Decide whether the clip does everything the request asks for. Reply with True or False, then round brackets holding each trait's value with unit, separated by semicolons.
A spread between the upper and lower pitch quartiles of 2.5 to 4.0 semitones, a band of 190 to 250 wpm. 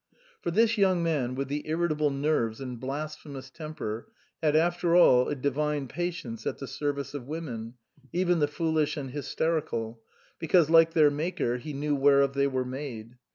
False (3.6 semitones; 165 wpm)